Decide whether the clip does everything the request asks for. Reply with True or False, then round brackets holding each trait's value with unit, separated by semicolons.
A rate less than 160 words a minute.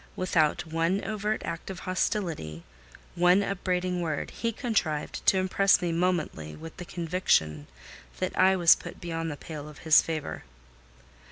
True (150 wpm)